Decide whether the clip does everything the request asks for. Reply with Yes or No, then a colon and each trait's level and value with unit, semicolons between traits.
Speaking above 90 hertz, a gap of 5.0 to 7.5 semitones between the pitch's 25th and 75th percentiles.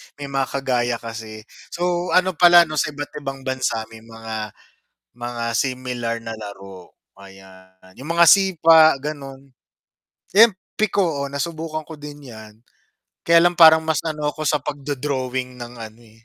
Yes: low, 135 Hz; wide, 5.5 semitones